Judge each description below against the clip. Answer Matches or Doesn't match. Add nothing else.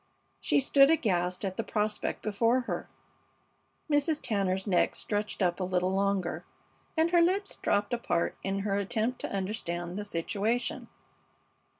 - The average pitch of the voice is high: Matches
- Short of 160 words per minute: Matches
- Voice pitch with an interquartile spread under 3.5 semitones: Doesn't match